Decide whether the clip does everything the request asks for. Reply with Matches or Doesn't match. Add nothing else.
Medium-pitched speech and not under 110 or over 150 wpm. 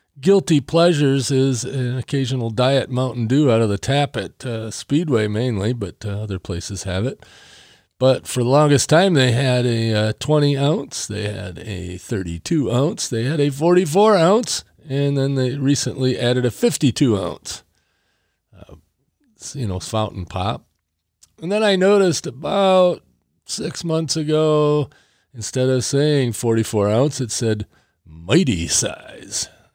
Doesn't match